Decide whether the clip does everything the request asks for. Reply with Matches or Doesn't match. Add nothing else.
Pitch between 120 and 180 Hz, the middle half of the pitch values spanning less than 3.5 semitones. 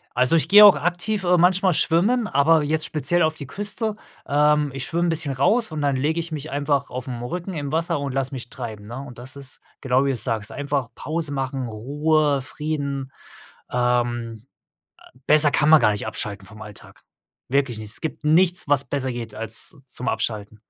Doesn't match